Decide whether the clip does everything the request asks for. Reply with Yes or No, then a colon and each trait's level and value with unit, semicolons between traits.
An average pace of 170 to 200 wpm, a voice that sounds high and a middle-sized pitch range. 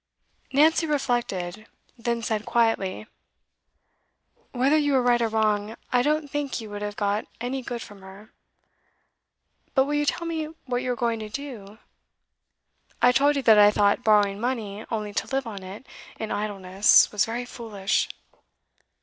No: average, 160 wpm; high, 230 Hz; average, 4.1 semitones